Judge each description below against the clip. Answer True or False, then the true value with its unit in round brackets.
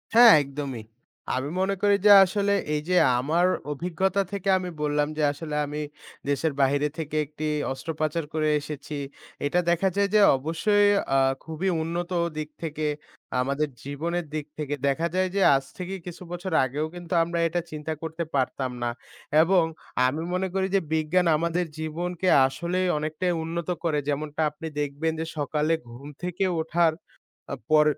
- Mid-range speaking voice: True (160 Hz)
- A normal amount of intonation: True (3.1 semitones)